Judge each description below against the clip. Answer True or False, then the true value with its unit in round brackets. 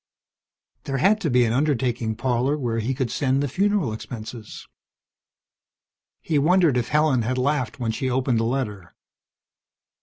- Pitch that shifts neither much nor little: True (3.7 semitones)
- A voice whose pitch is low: True (130 Hz)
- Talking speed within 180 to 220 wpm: False (150 wpm)